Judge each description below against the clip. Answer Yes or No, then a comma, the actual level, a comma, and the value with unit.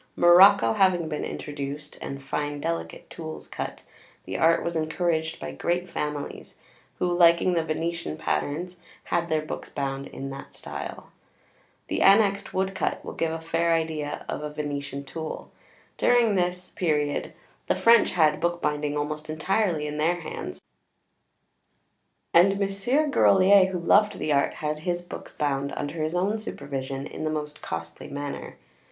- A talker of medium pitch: Yes, medium, 160 Hz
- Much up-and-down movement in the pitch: No, average, 3.3 semitones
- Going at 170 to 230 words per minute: No, average, 150 wpm